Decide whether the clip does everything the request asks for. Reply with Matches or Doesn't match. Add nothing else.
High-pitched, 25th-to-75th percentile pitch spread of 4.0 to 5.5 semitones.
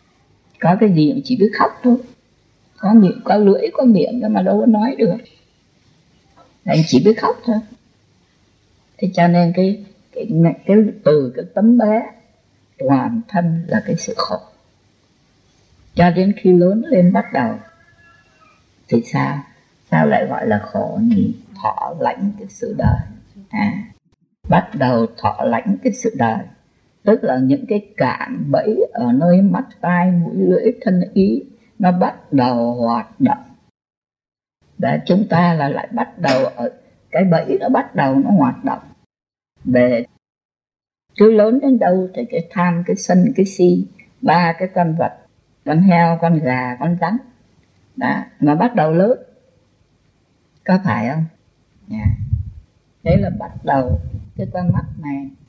Matches